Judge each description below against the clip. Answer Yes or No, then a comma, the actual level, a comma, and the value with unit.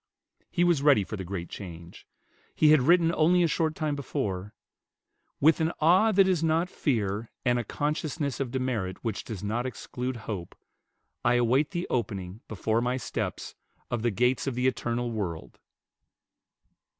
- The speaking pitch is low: Yes, low, 125 Hz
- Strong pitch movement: Yes, wide, 6.3 semitones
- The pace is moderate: Yes, average, 160 wpm